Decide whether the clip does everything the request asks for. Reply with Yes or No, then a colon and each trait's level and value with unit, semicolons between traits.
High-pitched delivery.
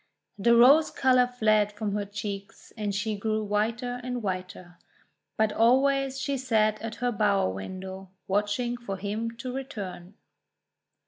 Yes: high, 215 Hz